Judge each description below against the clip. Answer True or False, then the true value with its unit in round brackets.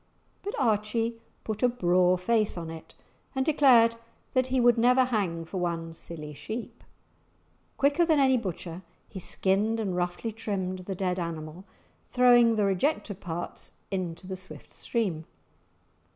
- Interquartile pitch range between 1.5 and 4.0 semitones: False (5.0 semitones)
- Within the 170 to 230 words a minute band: False (145 wpm)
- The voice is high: True (200 Hz)